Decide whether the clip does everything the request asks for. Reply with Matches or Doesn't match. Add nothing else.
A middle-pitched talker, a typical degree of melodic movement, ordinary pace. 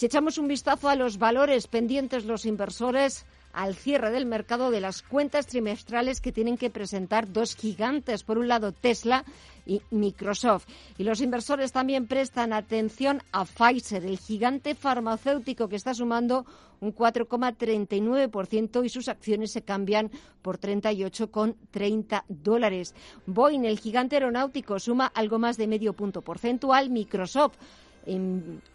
Doesn't match